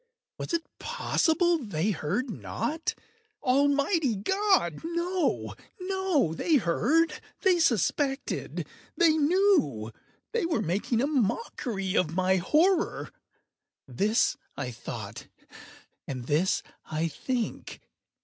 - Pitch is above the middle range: Yes, very high, 270 Hz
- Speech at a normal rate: No, slow, 85 wpm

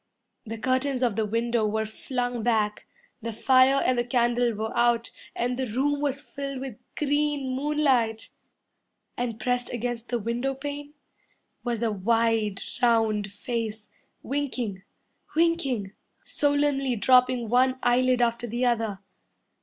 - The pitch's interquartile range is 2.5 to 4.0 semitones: Yes, average, 2.8 semitones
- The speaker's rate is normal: No, slow, 130 wpm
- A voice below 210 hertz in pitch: No, high, 245 Hz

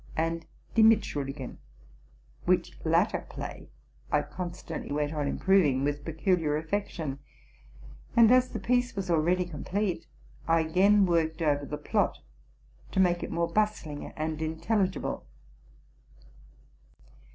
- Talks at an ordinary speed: No, slow, 125 wpm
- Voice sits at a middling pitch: Yes, medium, 165 Hz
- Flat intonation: No, average, 4.3 semitones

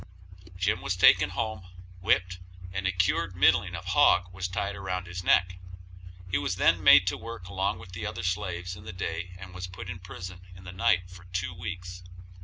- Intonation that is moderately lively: No, narrow, 0.8 semitones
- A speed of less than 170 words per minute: No, fast, 205 wpm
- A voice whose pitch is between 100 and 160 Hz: No, very low, 90 Hz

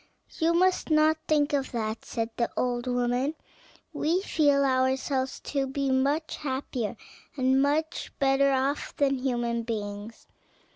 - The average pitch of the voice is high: Yes, very high, 270 Hz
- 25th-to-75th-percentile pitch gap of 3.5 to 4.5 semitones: No, average, 2.9 semitones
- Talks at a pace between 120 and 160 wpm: Yes, slow, 135 wpm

